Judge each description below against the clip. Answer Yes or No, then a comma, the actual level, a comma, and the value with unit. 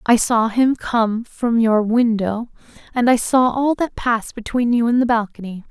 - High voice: Yes, high, 230 Hz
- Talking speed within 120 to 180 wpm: No, average, 190 wpm